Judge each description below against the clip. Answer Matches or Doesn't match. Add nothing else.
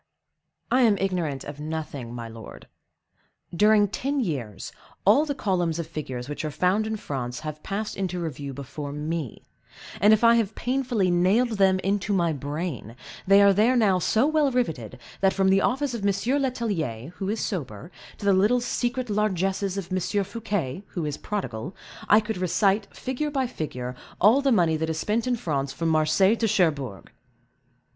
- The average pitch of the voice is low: Doesn't match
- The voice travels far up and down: Matches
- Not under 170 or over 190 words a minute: Matches